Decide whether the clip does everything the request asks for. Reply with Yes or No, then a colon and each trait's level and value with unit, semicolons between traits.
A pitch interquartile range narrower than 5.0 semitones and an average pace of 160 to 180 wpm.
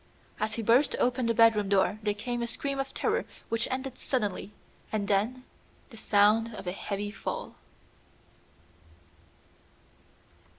No: average, 3.0 semitones; slow, 135 wpm